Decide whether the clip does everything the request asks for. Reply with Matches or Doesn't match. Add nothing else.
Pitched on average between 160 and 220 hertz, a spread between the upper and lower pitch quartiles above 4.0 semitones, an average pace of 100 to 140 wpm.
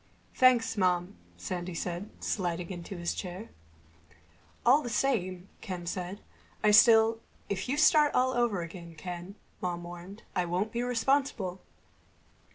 Matches